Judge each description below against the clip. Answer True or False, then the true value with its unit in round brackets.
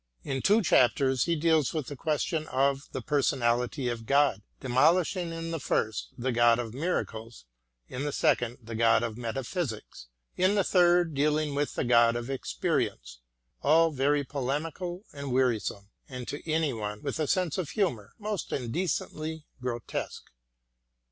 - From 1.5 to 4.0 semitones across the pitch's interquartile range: False (5.1 semitones)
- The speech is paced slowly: False (160 wpm)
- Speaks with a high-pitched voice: False (140 Hz)